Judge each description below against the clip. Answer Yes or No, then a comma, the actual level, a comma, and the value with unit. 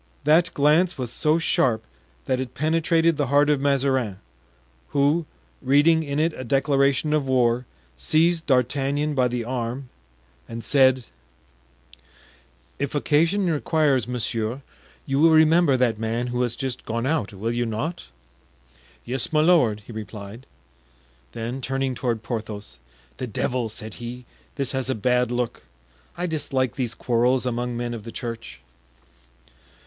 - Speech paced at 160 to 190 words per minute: No, average, 145 wpm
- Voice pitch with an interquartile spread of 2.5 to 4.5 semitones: Yes, average, 3.8 semitones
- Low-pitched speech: Yes, low, 130 Hz